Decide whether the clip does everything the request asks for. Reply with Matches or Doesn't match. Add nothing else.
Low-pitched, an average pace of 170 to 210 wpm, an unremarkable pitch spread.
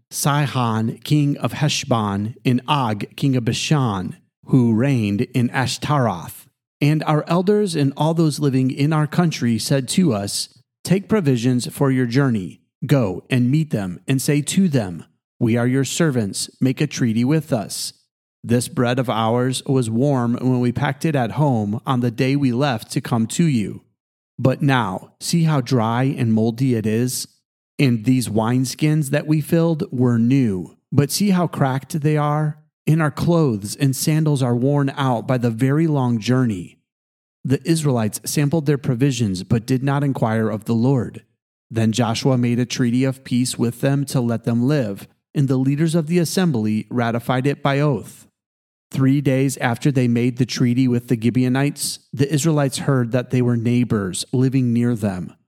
Matches